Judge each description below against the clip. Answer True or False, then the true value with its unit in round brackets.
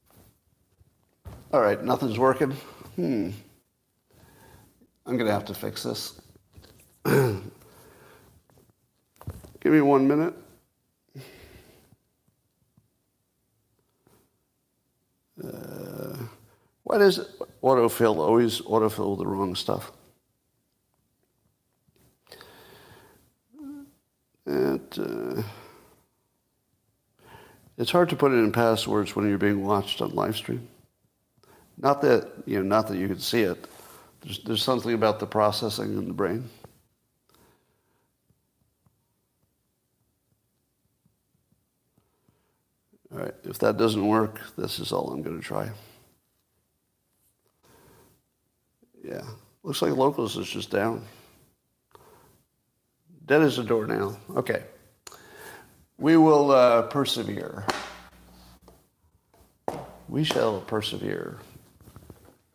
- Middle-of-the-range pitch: False (115 Hz)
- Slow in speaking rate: True (90 wpm)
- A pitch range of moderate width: True (4.8 semitones)